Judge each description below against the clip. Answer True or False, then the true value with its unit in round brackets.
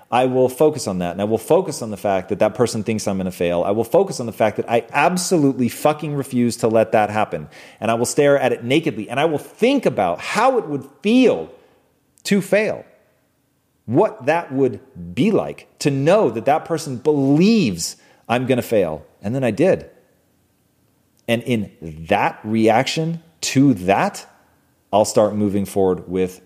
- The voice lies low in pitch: True (120 Hz)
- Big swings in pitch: True (6.2 semitones)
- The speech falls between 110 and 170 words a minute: False (190 wpm)